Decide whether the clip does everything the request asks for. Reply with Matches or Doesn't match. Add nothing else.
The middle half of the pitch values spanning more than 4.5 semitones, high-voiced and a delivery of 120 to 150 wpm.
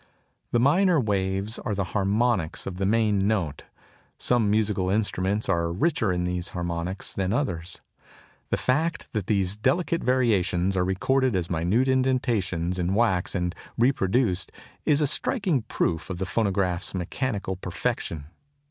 Doesn't match